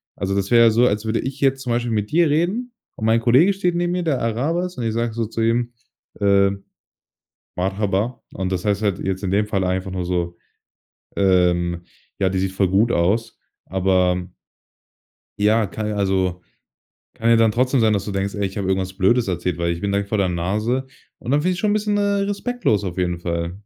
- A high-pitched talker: No, low, 105 Hz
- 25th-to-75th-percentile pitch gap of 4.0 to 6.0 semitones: Yes, average, 4.5 semitones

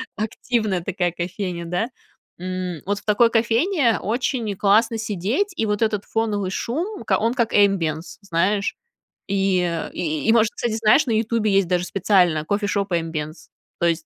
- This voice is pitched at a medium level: No, high, 200 Hz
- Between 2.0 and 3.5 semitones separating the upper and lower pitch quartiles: No, average, 4.0 semitones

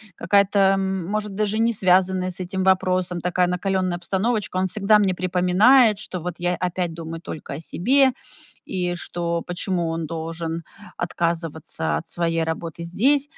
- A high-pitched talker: No, medium, 180 Hz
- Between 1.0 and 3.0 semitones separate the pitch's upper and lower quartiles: Yes, narrow, 2.5 semitones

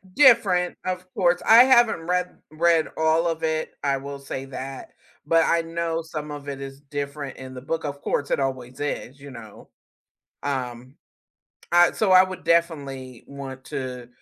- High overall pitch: No, medium, 145 Hz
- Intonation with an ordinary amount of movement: Yes, average, 3.9 semitones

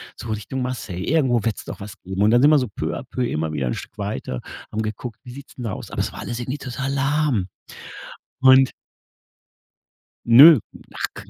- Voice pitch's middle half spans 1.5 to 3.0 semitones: No, average, 4.3 semitones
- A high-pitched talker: No, low, 120 Hz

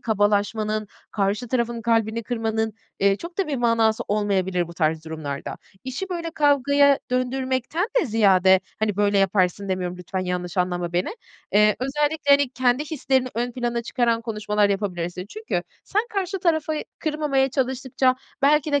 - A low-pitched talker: No, high, 230 Hz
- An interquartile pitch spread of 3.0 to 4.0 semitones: No, wide, 5.4 semitones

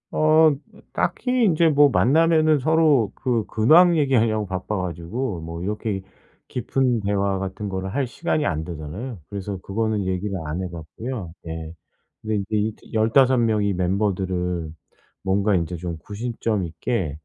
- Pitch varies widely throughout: Yes, wide, 5.8 semitones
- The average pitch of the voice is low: Yes, low, 105 Hz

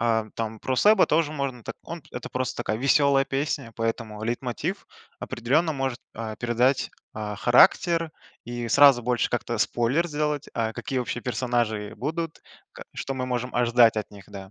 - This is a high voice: No, low, 125 Hz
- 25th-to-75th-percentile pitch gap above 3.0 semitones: Yes, average, 3.6 semitones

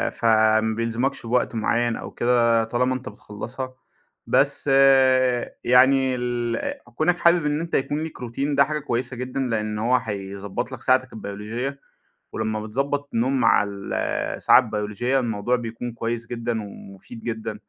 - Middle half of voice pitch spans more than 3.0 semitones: No, average, 2.7 semitones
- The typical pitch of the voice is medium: No, low, 120 Hz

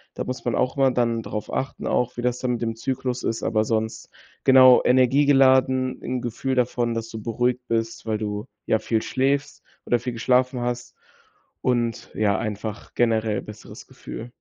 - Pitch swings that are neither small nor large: No, narrow, 2.2 semitones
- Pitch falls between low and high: No, low, 120 Hz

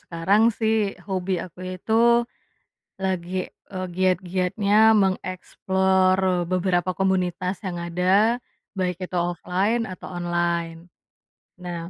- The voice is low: No, medium, 185 Hz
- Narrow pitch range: Yes, narrow, 1.2 semitones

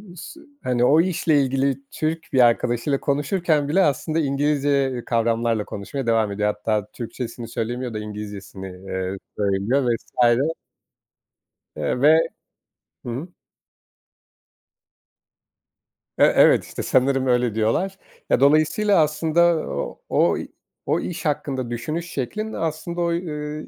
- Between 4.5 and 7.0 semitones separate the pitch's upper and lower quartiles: Yes, average, 5.1 semitones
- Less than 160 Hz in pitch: Yes, low, 135 Hz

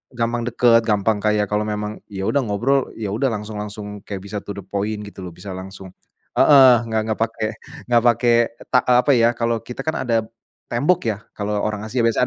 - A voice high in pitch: No, low, 110 Hz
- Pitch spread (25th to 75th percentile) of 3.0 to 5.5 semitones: No, narrow, 2.5 semitones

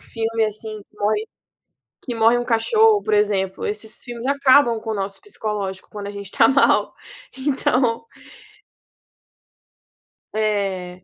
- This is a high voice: Yes, high, 220 Hz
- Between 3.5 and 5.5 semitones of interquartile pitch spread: No, average, 2.9 semitones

